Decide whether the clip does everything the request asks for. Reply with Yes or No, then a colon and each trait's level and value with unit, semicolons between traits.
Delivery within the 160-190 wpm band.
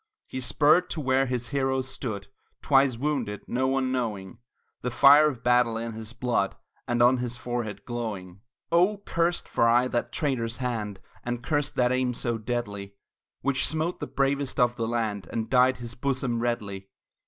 Yes: average, 170 wpm